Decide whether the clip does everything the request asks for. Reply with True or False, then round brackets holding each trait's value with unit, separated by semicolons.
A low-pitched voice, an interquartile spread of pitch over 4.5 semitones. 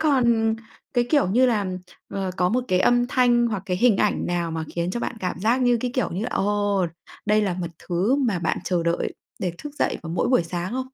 False (205 Hz; 5.2 semitones)